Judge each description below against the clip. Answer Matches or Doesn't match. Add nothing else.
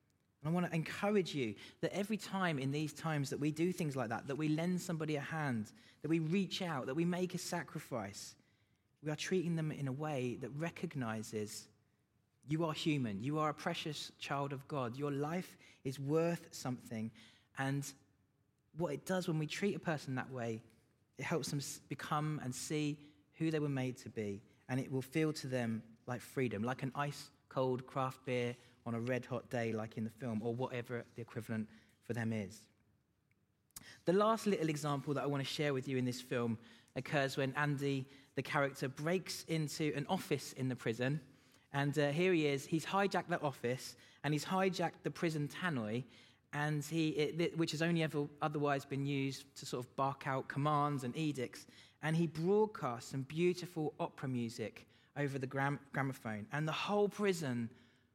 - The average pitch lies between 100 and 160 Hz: Matches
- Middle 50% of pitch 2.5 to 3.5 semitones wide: Doesn't match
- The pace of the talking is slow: Doesn't match